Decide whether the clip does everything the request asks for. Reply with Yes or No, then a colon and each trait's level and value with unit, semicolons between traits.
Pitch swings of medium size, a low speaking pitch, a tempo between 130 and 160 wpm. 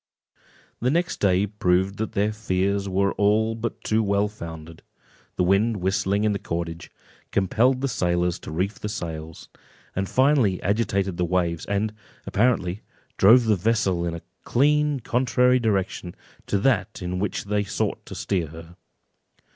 Yes: average, 3.7 semitones; low, 100 Hz; average, 150 wpm